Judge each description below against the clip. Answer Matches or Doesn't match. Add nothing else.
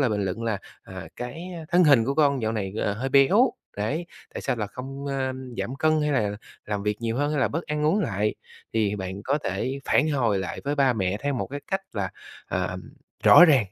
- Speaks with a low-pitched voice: Matches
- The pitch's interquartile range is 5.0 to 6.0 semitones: Matches